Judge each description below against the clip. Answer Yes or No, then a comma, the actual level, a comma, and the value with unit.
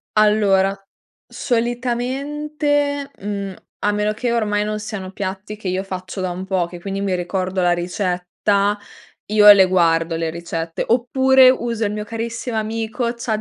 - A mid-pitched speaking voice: No, high, 210 Hz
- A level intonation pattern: No, average, 3.9 semitones